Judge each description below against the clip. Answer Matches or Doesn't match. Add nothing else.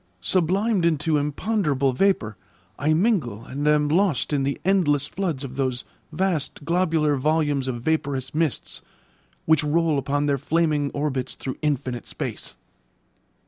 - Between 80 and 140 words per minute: Matches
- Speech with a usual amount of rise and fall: Matches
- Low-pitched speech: Doesn't match